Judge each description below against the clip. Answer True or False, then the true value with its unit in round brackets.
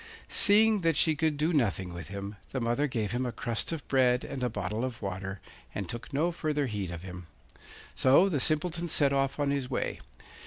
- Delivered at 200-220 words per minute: True (205 wpm)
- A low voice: True (130 Hz)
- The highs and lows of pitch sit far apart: True (6.6 semitones)